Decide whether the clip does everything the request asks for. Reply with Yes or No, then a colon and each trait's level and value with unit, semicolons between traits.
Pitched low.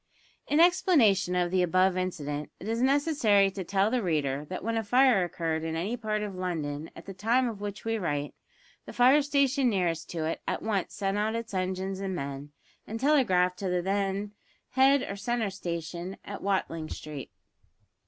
No: high, 195 Hz